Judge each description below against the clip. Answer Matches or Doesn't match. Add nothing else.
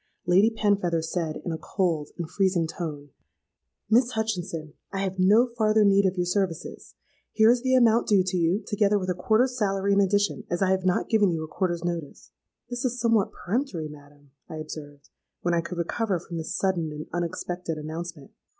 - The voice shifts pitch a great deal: Doesn't match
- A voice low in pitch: Doesn't match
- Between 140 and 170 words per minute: Doesn't match